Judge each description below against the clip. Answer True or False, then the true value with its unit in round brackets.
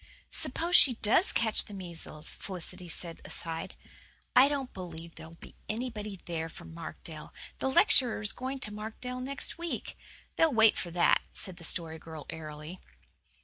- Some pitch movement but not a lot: False (7.1 semitones)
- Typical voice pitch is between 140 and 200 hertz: True (190 Hz)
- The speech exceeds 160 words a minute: False (155 wpm)